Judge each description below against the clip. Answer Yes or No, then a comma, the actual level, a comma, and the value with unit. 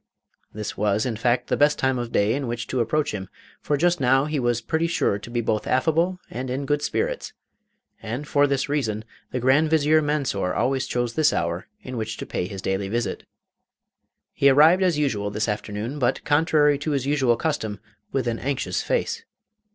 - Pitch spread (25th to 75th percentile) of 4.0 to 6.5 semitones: Yes, average, 5.1 semitones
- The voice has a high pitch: No, low, 130 Hz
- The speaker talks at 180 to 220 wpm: Yes, average, 195 wpm